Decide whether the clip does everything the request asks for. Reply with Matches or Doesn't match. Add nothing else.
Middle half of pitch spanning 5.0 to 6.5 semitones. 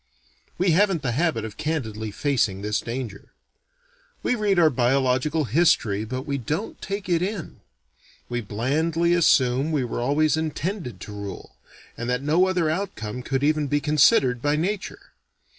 Matches